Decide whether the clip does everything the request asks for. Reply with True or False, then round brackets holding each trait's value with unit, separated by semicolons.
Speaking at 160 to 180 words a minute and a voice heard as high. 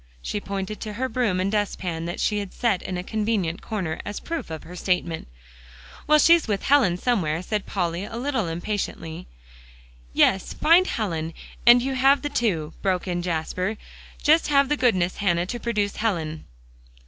True (170 wpm; 200 Hz)